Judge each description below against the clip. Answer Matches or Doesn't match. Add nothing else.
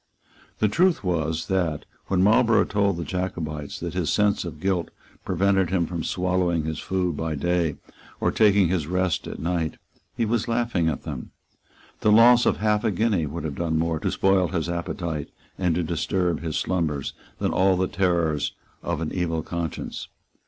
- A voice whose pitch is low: Matches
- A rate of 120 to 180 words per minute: Matches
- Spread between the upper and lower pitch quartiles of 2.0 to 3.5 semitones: Matches